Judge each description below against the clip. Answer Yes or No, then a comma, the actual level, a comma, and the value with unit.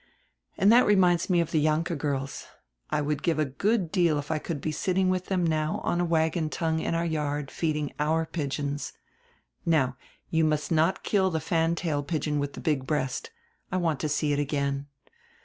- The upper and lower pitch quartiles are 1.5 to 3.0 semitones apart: Yes, narrow, 2.6 semitones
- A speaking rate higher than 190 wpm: Yes, average, 200 wpm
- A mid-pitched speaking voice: Yes, medium, 155 Hz